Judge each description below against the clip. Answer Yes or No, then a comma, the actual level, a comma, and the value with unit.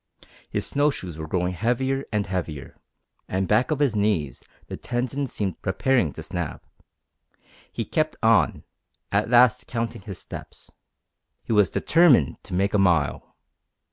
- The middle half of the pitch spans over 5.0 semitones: Yes, wide, 5.6 semitones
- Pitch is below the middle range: Yes, low, 105 Hz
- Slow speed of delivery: No, average, 145 wpm